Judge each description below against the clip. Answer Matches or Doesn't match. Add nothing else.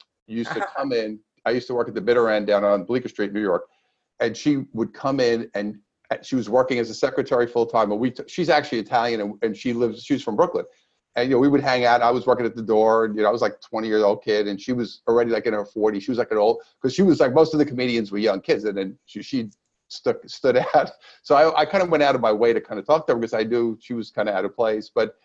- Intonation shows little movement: Doesn't match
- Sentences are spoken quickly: Matches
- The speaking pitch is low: Matches